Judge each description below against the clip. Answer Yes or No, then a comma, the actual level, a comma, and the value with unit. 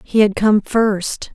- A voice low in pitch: No, high, 210 Hz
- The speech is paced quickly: No, average, 180 wpm